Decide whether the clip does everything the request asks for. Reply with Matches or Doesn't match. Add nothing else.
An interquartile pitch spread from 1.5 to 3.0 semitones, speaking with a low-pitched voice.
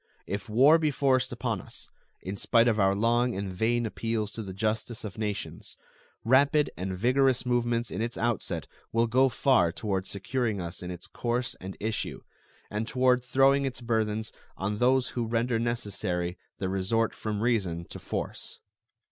Doesn't match